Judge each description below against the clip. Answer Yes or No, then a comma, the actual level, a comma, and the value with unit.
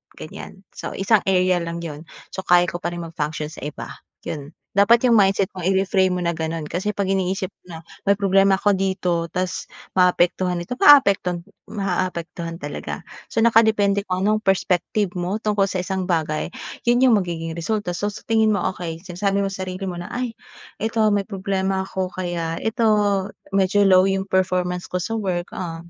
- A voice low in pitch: No, high, 190 Hz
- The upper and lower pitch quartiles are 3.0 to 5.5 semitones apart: No, narrow, 2.4 semitones